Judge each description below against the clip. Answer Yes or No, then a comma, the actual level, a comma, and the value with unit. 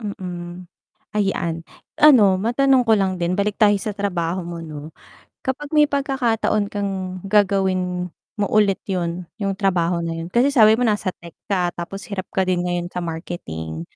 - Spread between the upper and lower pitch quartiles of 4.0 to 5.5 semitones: No, average, 3.3 semitones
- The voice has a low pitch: No, high, 190 Hz